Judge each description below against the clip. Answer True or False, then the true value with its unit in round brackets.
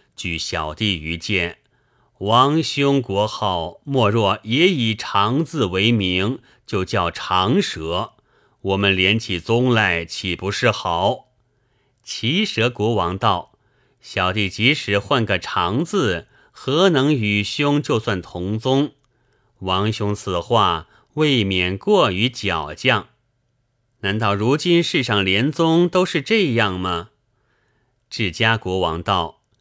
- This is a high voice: False (110 Hz)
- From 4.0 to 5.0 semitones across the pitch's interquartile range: True (4.7 semitones)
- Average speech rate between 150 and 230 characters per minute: True (160 characters per minute)